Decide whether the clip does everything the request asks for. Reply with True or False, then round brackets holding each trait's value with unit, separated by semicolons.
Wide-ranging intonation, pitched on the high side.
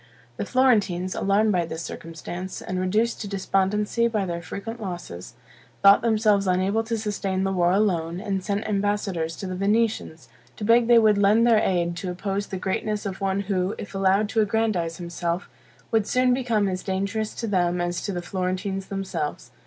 False (2.7 semitones; 195 Hz)